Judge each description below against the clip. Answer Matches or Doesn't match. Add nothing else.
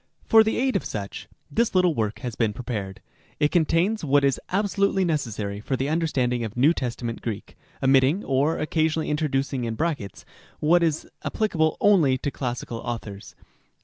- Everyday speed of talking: Matches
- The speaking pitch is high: Doesn't match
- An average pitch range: Doesn't match